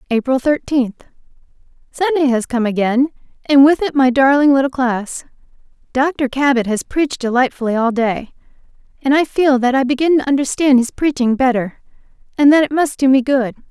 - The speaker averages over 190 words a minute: No, average, 160 wpm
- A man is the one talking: No, female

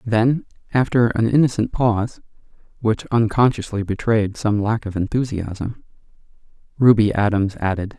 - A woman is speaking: No, male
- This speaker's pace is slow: Yes, slow, 115 wpm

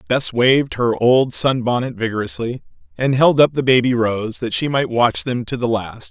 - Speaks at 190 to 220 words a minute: Yes, fast, 205 wpm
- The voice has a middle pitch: No, low, 120 Hz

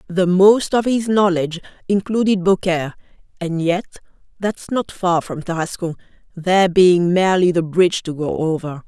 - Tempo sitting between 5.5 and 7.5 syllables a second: No, 5.0 syllables/s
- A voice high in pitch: No, medium, 180 Hz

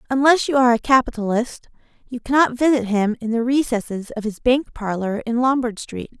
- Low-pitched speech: No, high, 240 Hz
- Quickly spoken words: No, average, 185 wpm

